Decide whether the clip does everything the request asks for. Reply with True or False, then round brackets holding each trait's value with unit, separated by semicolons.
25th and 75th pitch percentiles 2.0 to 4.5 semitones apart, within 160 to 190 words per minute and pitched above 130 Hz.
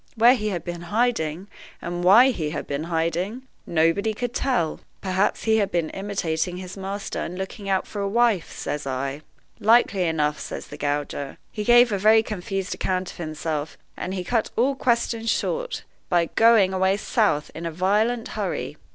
False (4.9 semitones; 175 wpm; 190 Hz)